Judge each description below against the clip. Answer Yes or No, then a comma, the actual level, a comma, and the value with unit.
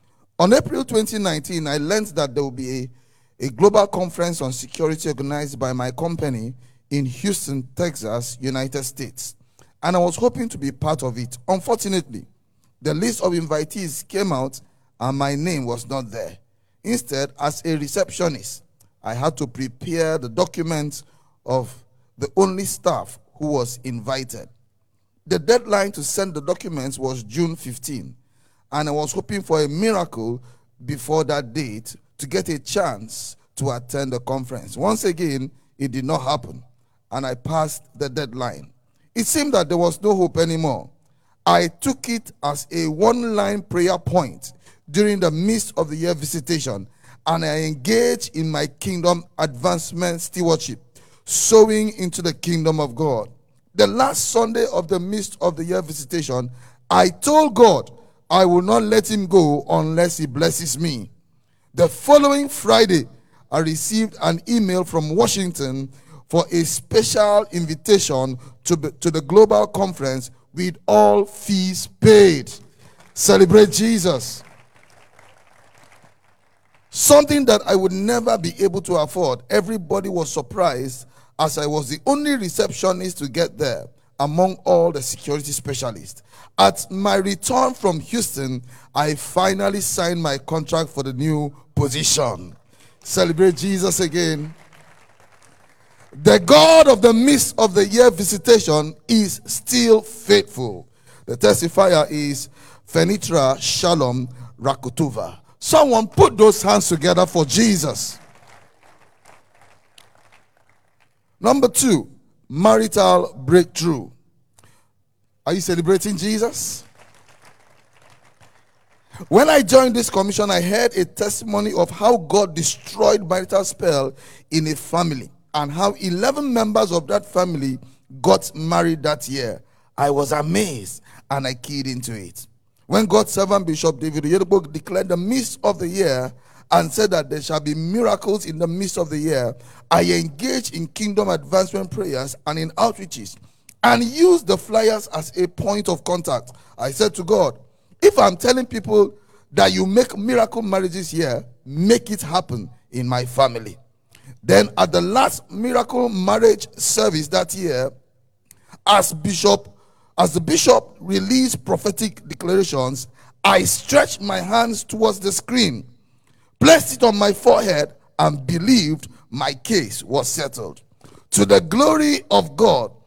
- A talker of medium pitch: Yes, medium, 160 Hz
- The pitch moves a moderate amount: No, wide, 6.9 semitones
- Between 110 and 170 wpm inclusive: Yes, average, 140 wpm